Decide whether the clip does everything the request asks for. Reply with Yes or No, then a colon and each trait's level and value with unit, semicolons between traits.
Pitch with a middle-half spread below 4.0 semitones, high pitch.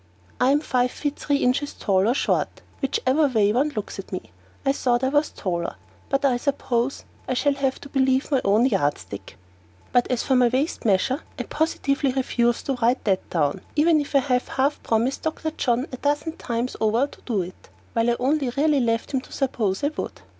Yes: average, 3.5 semitones; very high, 255 Hz